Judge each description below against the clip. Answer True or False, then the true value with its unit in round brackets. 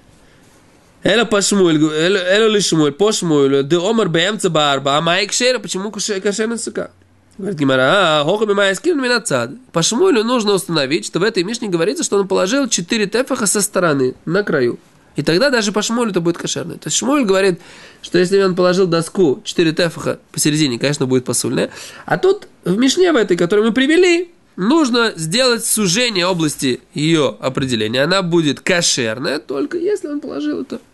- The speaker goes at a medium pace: True (145 wpm)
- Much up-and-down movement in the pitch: True (6.1 semitones)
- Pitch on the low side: False (195 Hz)